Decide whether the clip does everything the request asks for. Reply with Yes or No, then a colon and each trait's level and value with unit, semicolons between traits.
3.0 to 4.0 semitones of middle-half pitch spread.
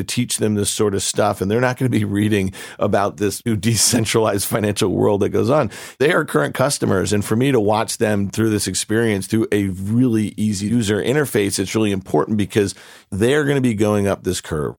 No: narrow, 2.4 semitones